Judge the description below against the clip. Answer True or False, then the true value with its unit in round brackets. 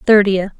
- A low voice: False (200 Hz)